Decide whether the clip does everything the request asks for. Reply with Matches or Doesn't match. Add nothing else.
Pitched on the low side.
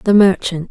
Doesn't match